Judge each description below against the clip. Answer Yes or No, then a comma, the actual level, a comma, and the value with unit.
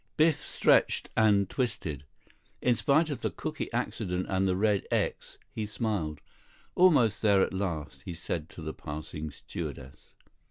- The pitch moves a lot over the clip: Yes, wide, 6.0 semitones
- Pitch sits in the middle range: No, very low, 95 Hz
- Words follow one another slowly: No, average, 150 wpm